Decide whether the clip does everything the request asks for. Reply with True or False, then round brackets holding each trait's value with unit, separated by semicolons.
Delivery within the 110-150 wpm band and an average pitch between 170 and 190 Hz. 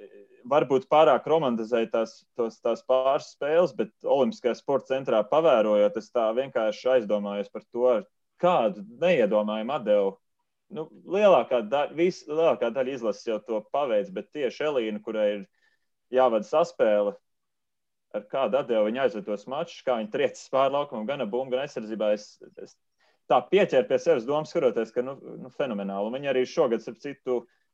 False (140 wpm; 130 Hz)